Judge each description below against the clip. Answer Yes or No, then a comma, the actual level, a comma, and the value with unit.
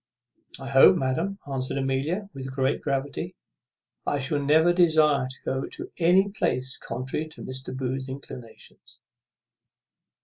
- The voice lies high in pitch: No, low, 135 Hz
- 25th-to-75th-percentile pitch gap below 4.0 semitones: Yes, average, 3.2 semitones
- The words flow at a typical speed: No, slow, 130 wpm